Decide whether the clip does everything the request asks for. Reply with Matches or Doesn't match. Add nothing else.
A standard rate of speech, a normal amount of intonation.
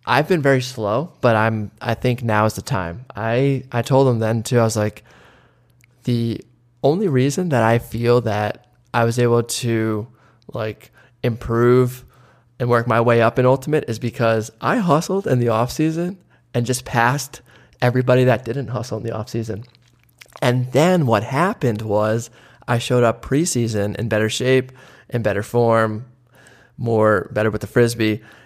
Doesn't match